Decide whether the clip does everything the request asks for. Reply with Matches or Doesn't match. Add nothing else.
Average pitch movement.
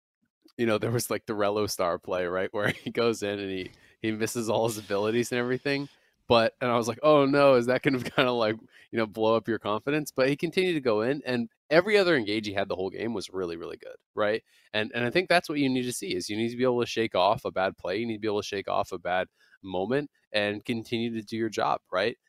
Matches